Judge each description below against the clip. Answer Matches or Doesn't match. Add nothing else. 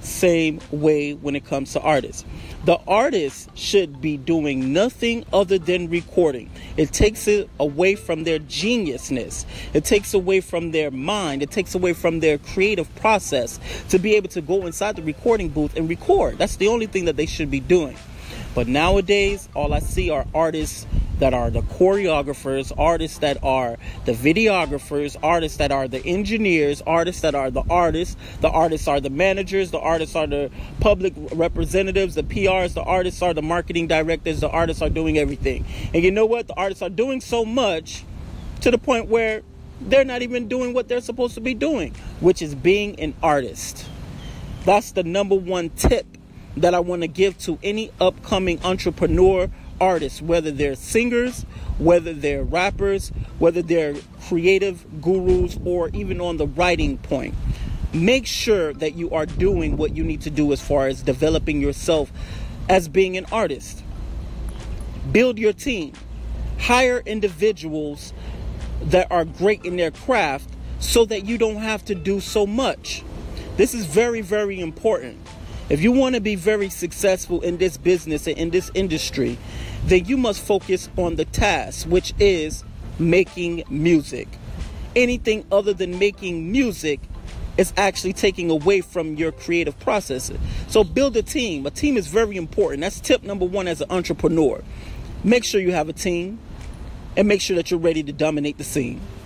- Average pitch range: Matches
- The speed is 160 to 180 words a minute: Matches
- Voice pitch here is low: Doesn't match